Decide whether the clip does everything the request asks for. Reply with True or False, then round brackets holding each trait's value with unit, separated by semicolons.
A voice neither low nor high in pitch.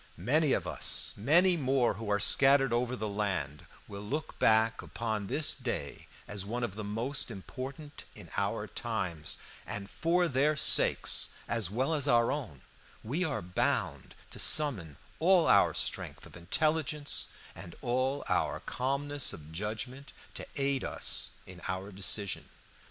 False (120 Hz)